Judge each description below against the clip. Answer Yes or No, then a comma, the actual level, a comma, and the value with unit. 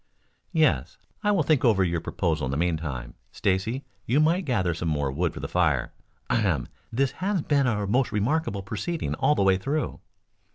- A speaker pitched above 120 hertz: No, low, 100 Hz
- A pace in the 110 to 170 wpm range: No, average, 180 wpm